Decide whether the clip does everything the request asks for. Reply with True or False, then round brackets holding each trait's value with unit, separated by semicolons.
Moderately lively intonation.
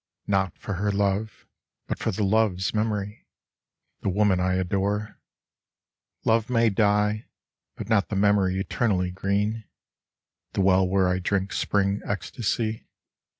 False (2.0 semitones)